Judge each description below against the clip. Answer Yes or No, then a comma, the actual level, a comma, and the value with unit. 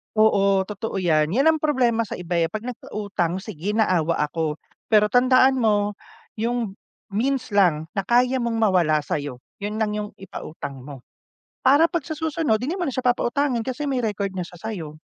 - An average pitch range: No, wide, 5.9 semitones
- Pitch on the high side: Yes, high, 215 Hz